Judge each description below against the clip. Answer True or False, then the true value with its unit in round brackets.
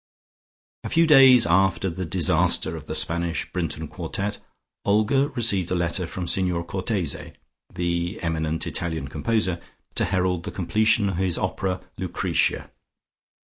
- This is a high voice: False (90 Hz)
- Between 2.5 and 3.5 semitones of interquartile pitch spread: True (3.2 semitones)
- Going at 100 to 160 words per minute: True (135 wpm)